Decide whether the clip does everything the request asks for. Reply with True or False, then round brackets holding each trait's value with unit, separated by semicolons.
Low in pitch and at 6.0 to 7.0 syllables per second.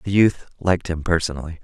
True (85 Hz; 6.2 syllables/s)